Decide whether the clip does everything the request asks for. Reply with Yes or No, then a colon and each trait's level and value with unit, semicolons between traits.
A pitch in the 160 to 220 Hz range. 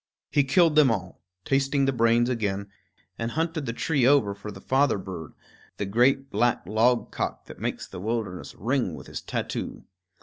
No: low, 120 Hz